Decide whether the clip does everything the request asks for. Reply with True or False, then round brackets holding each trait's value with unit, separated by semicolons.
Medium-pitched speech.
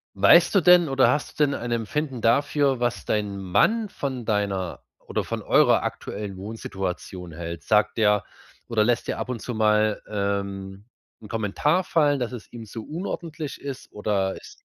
False (110 Hz)